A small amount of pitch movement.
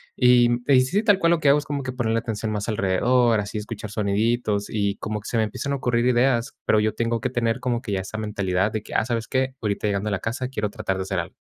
No: average, 3.0 semitones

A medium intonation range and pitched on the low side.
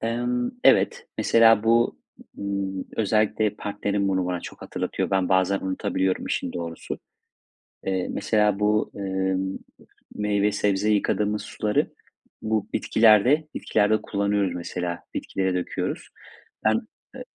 No: narrow, 2.1 semitones; low, 100 Hz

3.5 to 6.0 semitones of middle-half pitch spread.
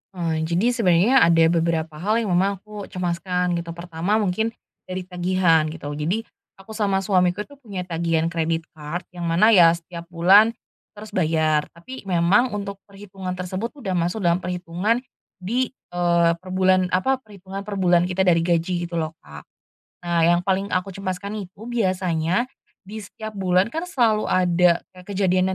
No: average, 2.8 semitones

